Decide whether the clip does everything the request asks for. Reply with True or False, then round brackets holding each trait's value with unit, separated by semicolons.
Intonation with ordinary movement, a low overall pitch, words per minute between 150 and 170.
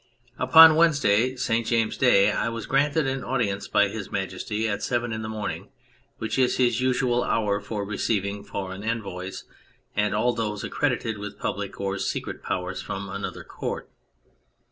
True (3.5 semitones; 110 Hz; 160 wpm)